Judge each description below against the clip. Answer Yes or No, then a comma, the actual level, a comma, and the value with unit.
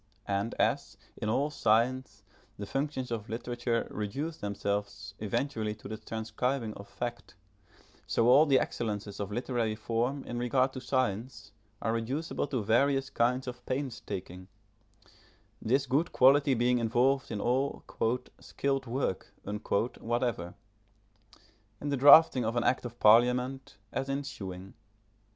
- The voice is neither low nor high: No, low, 120 Hz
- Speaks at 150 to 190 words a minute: No, slow, 135 wpm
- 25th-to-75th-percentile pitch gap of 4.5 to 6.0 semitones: No, average, 3.7 semitones